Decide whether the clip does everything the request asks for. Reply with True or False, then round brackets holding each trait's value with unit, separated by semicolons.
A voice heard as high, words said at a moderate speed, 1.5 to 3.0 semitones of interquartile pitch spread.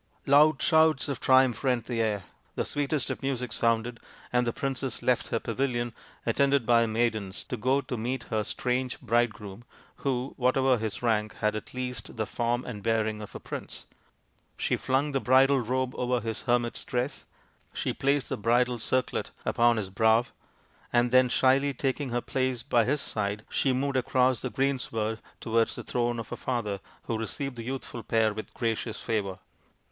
False (120 Hz; 175 wpm; 2.6 semitones)